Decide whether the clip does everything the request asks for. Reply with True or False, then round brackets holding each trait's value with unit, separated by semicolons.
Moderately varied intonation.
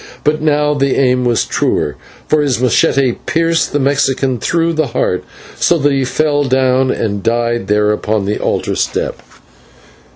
True (3.9 semitones)